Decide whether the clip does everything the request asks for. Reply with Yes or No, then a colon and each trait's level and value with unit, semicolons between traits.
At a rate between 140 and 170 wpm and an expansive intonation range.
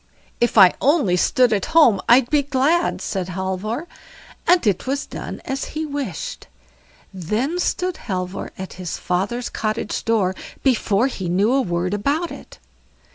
Yes: average, 155 wpm; wide, 6.8 semitones